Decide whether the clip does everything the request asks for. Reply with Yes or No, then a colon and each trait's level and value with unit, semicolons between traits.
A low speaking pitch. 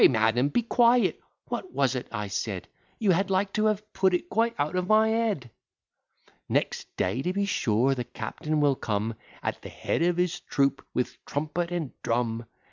No: medium, 155 Hz